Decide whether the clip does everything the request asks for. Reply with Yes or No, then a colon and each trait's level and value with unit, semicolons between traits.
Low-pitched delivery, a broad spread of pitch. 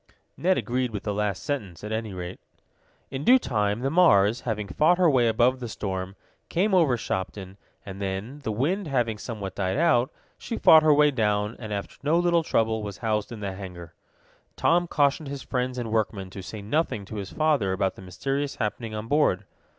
Yes: low, 110 Hz; wide, 6.0 semitones